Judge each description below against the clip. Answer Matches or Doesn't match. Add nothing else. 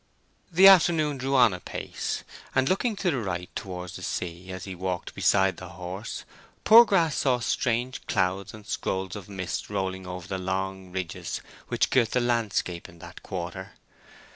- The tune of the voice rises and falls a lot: Matches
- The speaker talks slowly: Doesn't match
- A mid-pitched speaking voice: Doesn't match